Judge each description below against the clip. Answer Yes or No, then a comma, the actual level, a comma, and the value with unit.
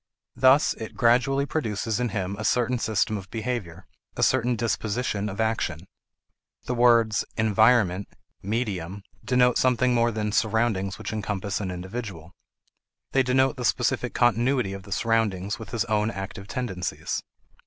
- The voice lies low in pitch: Yes, low, 110 Hz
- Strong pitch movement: No, average, 3.6 semitones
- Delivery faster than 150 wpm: No, average, 145 wpm